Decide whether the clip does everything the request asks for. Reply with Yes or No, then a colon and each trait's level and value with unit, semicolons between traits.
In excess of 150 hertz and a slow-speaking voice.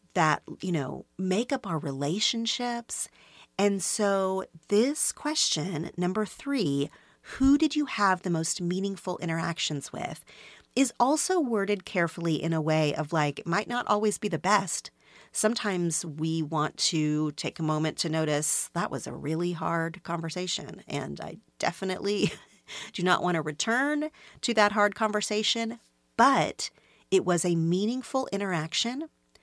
No: high, 190 Hz; average, 145 wpm